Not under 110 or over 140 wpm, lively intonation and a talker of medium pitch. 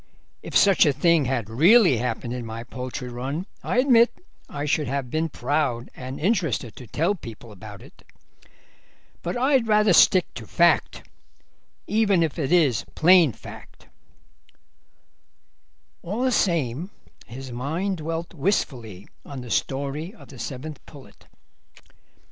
Yes: slow, 135 wpm; wide, 6.2 semitones; medium, 145 Hz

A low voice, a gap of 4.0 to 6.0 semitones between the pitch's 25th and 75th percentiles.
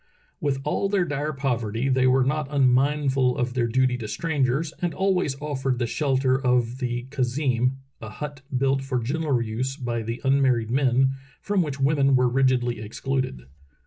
No: low, 130 Hz; narrow, 2.4 semitones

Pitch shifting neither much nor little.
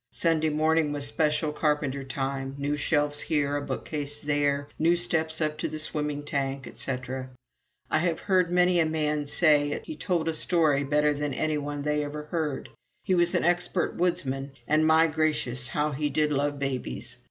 No: narrow, 1.9 semitones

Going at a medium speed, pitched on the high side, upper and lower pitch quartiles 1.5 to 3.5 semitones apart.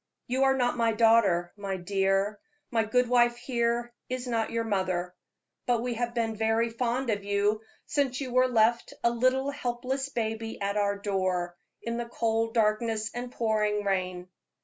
Yes: average, 170 wpm; high, 225 Hz; average, 2.9 semitones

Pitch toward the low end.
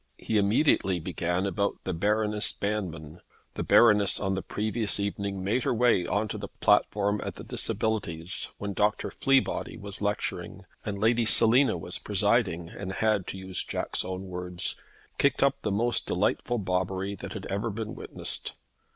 Yes: low, 100 Hz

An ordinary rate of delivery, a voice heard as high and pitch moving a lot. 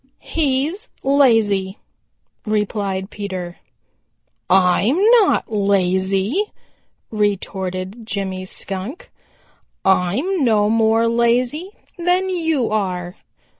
No: slow, 75 wpm; high, 210 Hz; wide, 5.8 semitones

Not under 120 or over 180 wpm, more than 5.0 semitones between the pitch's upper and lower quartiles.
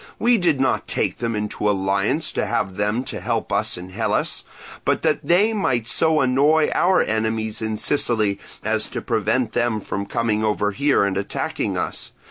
Yes: average, 175 wpm; wide, 5.6 semitones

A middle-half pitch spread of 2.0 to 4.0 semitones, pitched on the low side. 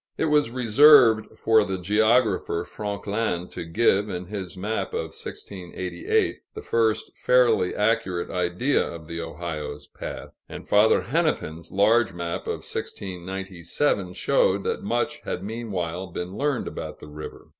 No: average, 4.5 semitones; low, 100 Hz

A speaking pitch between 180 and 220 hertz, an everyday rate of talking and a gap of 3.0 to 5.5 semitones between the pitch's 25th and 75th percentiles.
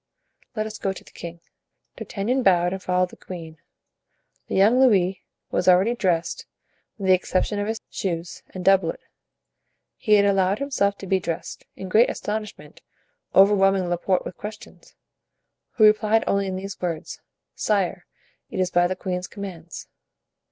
No: high, 190 Hz; average, 155 wpm; narrow, 2.5 semitones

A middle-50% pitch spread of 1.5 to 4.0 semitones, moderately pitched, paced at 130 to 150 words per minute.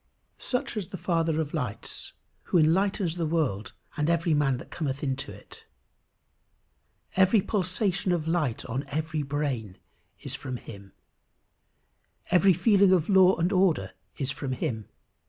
No: average, 5.1 semitones; medium, 160 Hz; average, 140 wpm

